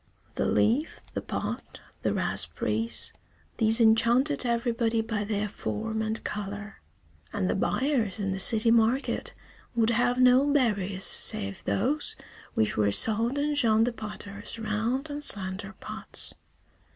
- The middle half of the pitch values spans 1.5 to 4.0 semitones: Yes, average, 3.1 semitones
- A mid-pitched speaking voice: No, high, 225 Hz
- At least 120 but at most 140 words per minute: Yes, slow, 135 wpm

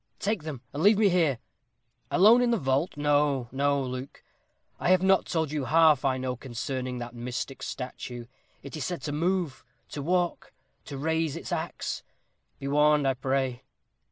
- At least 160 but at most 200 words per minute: Yes, average, 170 wpm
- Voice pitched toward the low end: No, medium, 145 Hz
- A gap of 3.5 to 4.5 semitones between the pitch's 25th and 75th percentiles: Yes, average, 4.1 semitones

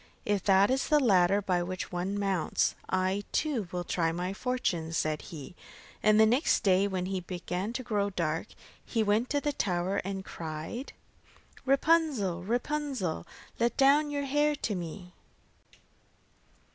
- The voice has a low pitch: No, high, 200 Hz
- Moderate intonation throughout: No, wide, 5.9 semitones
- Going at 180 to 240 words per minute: No, average, 150 wpm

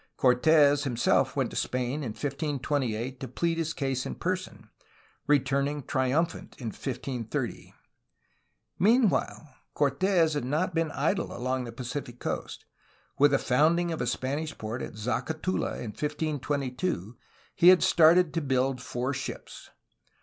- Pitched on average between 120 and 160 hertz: Yes, medium, 140 Hz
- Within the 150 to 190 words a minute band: No, slow, 135 wpm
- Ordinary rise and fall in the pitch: Yes, average, 3.9 semitones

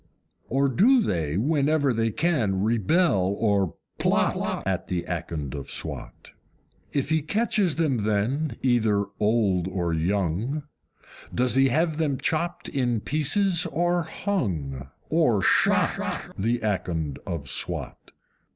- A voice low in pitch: Yes, low, 120 Hz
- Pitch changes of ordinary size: No, wide, 8.7 semitones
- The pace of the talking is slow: Yes, slow, 125 wpm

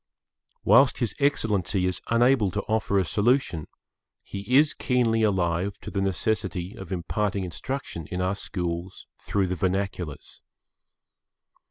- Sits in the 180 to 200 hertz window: No, low, 100 Hz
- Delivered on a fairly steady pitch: No, average, 3.6 semitones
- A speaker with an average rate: No, slow, 130 wpm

